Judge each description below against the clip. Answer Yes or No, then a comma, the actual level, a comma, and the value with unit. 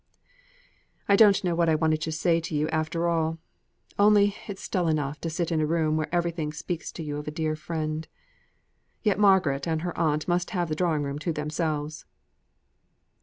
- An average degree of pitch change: No, narrow, 2.1 semitones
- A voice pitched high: No, medium, 160 Hz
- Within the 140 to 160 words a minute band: No, average, 190 wpm